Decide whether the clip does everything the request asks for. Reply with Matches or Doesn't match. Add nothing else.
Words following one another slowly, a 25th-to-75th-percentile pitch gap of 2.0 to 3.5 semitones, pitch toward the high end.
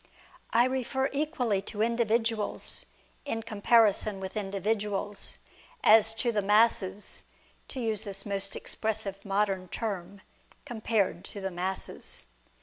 Matches